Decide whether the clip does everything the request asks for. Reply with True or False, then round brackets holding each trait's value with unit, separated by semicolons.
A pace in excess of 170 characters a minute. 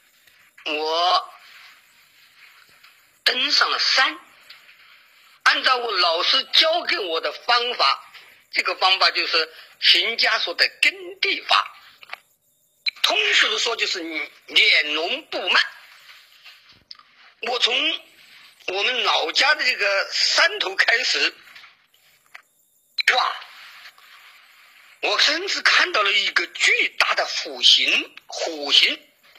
False (140 characters per minute)